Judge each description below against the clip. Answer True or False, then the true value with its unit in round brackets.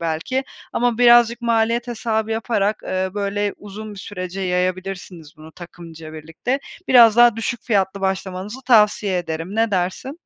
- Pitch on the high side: True (205 Hz)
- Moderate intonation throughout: True (4.0 semitones)